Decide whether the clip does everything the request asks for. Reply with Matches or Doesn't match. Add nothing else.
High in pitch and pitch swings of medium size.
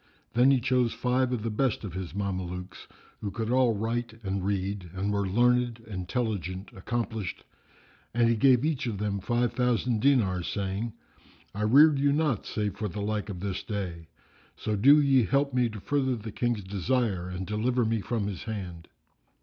Doesn't match